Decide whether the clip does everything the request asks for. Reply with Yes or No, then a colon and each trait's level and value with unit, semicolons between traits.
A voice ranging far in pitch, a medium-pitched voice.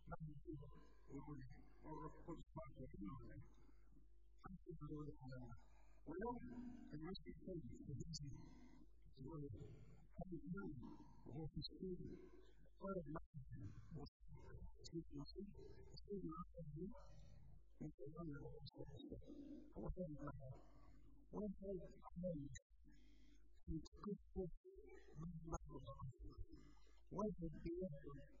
No: average, 4.7 semitones; medium, 160 Hz